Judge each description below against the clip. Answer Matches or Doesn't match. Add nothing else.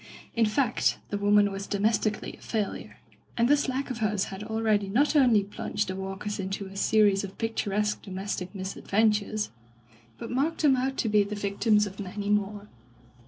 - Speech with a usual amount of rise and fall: Doesn't match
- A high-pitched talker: Matches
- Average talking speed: Matches